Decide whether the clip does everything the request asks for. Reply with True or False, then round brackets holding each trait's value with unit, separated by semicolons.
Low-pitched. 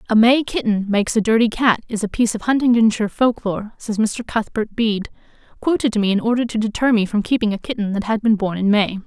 False (220 Hz)